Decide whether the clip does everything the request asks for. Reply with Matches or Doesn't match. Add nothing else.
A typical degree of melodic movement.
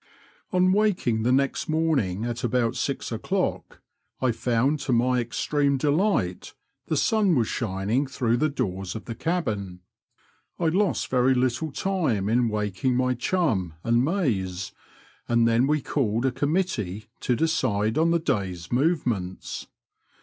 Doesn't match